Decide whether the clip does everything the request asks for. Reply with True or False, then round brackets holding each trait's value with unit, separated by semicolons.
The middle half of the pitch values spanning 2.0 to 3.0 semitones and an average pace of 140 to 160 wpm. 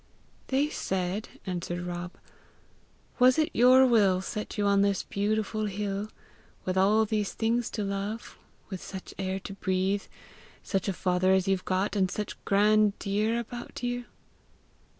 True (2.4 semitones; 150 wpm)